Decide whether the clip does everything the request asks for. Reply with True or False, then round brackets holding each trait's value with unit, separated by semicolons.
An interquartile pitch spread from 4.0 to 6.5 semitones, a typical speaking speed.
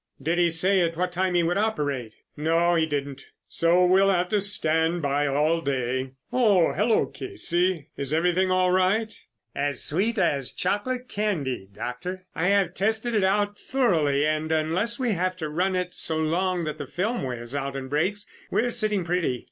True (4.6 semitones; 180 wpm)